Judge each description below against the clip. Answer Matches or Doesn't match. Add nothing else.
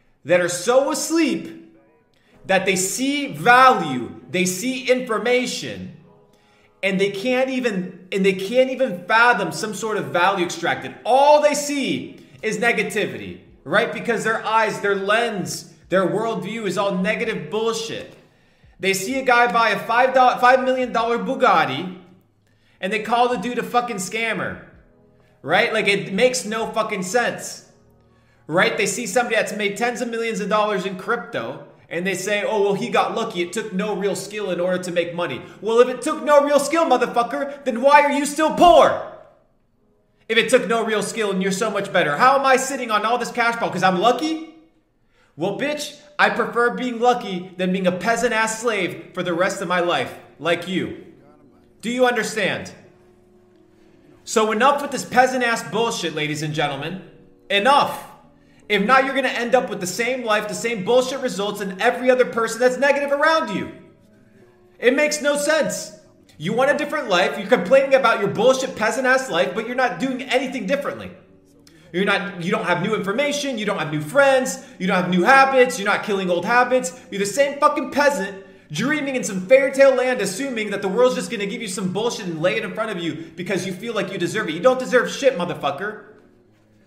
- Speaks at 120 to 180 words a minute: Doesn't match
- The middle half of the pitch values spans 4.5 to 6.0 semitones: Matches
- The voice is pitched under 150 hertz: Doesn't match